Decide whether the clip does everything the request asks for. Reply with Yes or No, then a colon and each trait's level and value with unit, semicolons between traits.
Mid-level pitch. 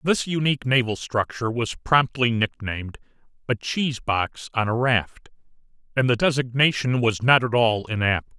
No: low, 120 Hz